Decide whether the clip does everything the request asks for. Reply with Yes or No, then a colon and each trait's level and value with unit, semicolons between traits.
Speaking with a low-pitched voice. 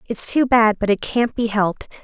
No: high, 225 Hz